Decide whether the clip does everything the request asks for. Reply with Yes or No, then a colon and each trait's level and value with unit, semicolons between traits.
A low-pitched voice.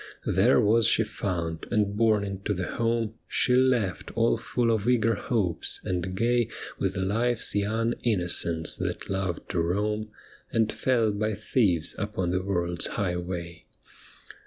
Yes: low, 105 Hz